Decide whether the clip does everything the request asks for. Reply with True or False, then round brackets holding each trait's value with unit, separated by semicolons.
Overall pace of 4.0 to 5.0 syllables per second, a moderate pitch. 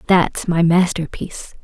True (4.3 syllables/s; 170 Hz)